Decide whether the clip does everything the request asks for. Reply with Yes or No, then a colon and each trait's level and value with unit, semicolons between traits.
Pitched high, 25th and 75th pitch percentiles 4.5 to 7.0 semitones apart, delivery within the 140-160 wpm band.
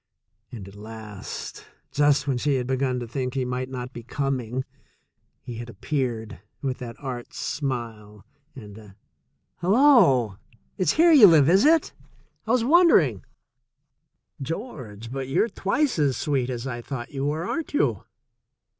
No: low, 130 Hz; average, 4.9 semitones; average, 150 wpm